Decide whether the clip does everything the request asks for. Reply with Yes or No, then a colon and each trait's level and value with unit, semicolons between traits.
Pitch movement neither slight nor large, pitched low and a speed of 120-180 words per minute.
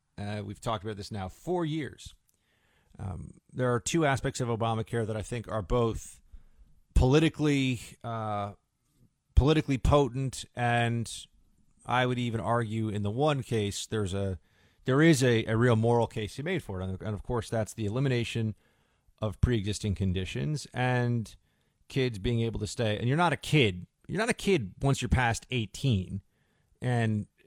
Yes: average, 3.8 semitones; low, 115 Hz; average, 165 wpm